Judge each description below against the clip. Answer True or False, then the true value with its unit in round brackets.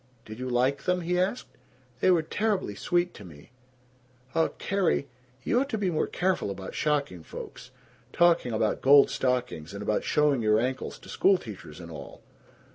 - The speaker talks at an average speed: True (170 wpm)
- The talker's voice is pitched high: False (140 Hz)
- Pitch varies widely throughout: True (8.8 semitones)